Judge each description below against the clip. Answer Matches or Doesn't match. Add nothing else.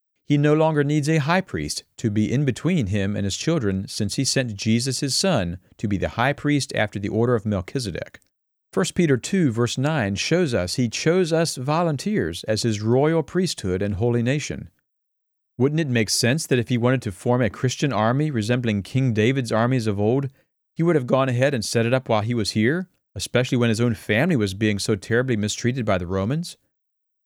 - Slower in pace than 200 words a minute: Doesn't match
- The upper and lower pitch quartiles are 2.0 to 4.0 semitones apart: Doesn't match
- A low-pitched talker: Matches